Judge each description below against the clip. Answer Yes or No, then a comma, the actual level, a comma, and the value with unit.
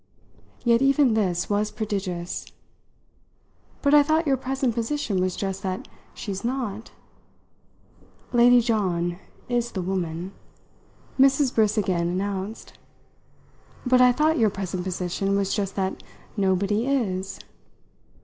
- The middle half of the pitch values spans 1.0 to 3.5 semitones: No, average, 4.6 semitones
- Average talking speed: No, slow, 120 wpm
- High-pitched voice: Yes, high, 205 Hz